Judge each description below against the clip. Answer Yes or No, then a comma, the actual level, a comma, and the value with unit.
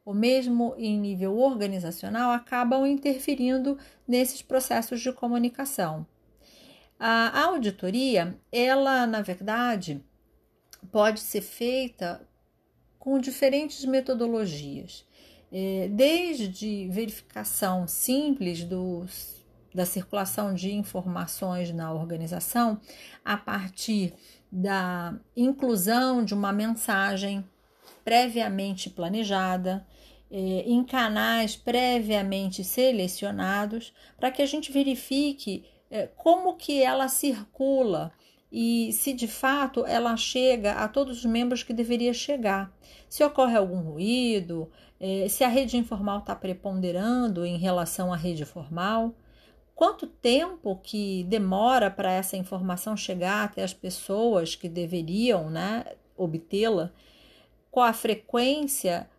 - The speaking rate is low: Yes, slow, 105 wpm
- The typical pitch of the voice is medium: No, high, 220 Hz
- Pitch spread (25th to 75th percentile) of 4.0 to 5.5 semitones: Yes, average, 5.0 semitones